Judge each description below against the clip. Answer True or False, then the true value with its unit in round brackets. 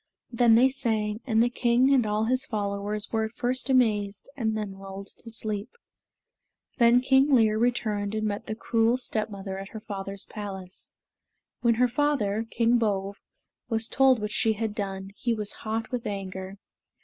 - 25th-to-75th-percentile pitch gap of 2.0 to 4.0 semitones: True (2.8 semitones)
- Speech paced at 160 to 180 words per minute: True (170 wpm)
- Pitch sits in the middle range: False (220 Hz)